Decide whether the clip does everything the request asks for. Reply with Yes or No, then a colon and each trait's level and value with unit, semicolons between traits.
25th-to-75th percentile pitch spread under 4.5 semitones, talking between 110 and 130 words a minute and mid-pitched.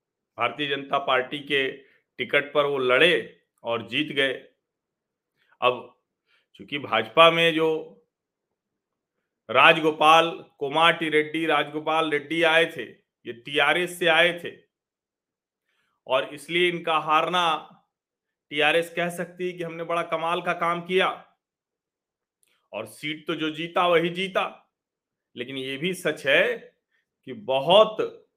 Yes: average, 2.8 semitones; average, 120 wpm; medium, 160 Hz